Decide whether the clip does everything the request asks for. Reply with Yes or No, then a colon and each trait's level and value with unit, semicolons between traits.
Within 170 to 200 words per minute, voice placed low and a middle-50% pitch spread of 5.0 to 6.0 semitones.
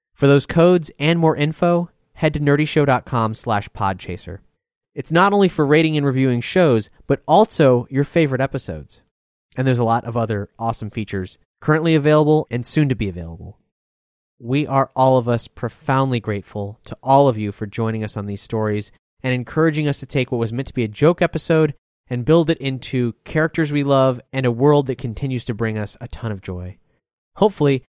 Yes: average, 190 wpm; low, 130 Hz; wide, 5.6 semitones